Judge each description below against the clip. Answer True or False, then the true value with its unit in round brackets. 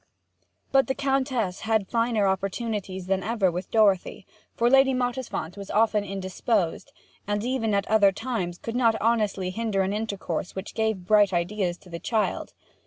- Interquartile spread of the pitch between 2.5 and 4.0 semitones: True (3.3 semitones)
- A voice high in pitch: True (210 Hz)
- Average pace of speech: True (160 wpm)